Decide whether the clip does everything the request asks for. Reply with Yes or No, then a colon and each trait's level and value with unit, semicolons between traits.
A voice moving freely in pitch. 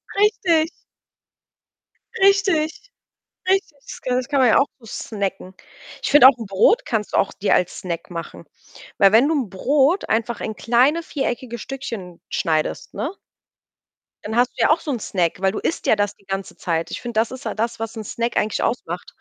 Yes: wide, 5.9 semitones